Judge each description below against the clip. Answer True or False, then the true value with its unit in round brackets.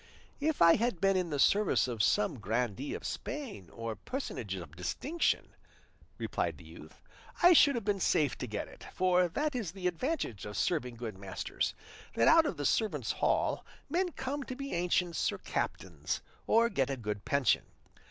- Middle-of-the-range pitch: True (170 Hz)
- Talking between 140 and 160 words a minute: False (180 wpm)